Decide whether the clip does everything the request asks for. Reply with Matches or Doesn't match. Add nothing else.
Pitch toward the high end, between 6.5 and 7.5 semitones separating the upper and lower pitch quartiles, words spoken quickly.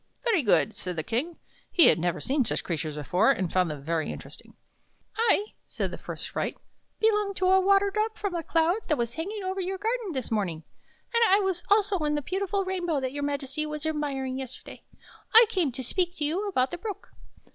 Matches